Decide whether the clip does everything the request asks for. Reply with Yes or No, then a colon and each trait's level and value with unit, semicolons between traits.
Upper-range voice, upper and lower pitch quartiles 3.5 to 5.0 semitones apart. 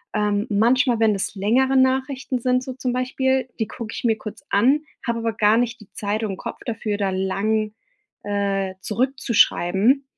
Yes: high, 225 Hz; average, 3.8 semitones